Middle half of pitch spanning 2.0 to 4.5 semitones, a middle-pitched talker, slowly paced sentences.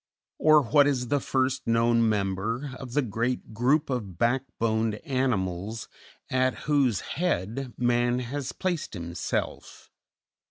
No: average, 3.3 semitones; low, 120 Hz; slow, 120 wpm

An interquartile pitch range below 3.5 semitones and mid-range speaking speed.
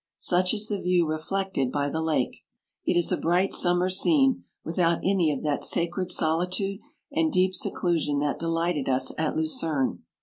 Yes: average, 3.0 semitones; average, 175 wpm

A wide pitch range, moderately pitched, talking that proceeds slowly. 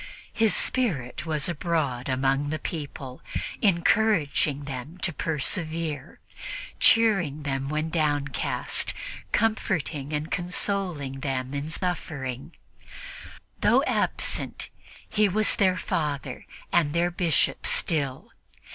No: average, 4.2 semitones; medium, 155 Hz; slow, 100 wpm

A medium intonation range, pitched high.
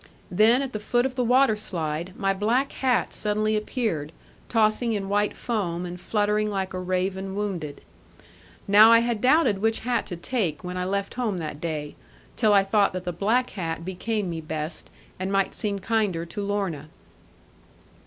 Yes: average, 3.6 semitones; high, 200 Hz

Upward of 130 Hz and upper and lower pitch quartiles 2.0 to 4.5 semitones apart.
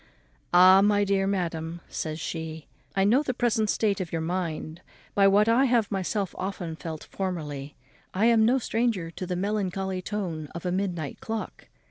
Yes: high, 190 Hz; average, 3.9 semitones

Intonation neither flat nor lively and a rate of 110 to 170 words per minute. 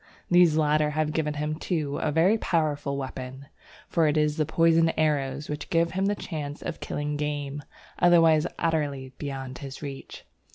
No: narrow, 2.3 semitones; average, 165 wpm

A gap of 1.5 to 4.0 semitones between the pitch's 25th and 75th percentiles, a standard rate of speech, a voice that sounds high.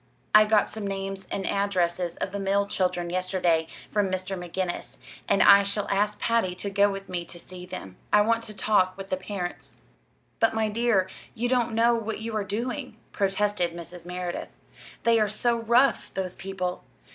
Yes: average, 2.7 semitones; average, 180 wpm; high, 195 Hz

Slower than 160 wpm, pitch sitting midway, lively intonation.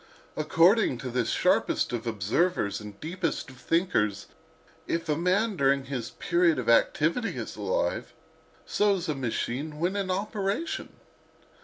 Yes: average, 140 wpm; medium, 155 Hz; wide, 6.7 semitones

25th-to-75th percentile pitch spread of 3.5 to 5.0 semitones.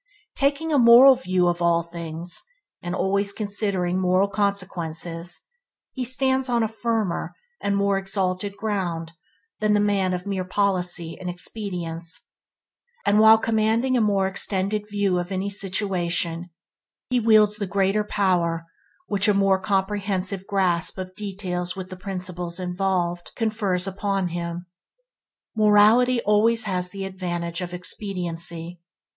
No: average, 2.7 semitones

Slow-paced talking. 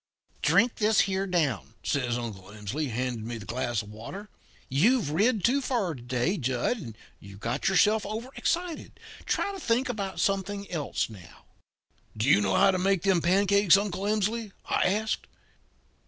No: average, 165 wpm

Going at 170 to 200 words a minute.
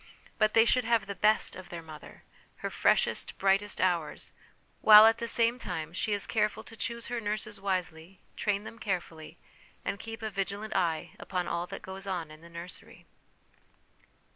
Yes: average, 175 wpm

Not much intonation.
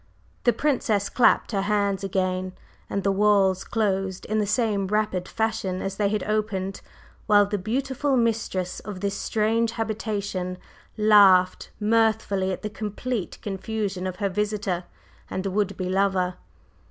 Yes: narrow, 2.3 semitones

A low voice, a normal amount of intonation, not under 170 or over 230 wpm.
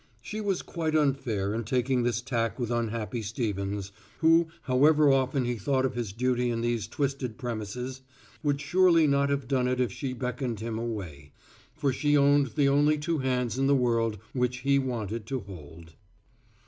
Yes: low, 125 Hz; average, 3.4 semitones; average, 175 wpm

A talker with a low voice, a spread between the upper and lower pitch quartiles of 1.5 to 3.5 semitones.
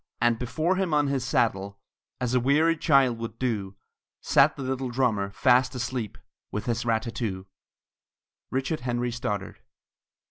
Yes: low, 125 Hz; average, 2.9 semitones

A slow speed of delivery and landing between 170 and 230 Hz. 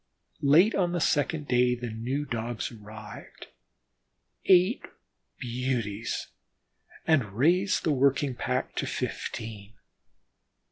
No: slow, 100 wpm; low, 125 Hz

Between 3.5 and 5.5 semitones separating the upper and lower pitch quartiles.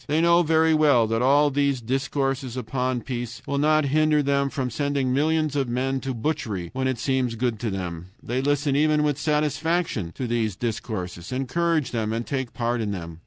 Yes: average, 4.0 semitones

